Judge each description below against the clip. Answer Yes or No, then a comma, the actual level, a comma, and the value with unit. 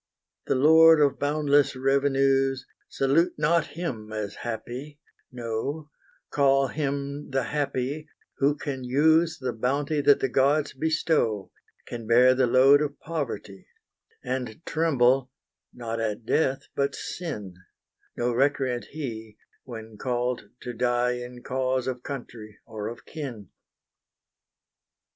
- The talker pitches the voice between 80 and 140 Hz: Yes, low, 135 Hz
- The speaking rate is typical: No, slow, 120 wpm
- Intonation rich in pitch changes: No, average, 3.1 semitones